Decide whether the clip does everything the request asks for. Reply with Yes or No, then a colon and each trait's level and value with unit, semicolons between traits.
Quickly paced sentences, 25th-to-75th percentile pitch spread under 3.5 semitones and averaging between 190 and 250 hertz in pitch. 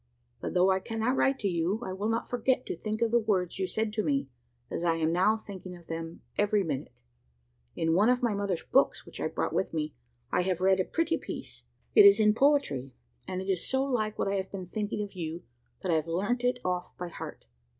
No: fast, 235 wpm; average, 4.2 semitones; high, 195 Hz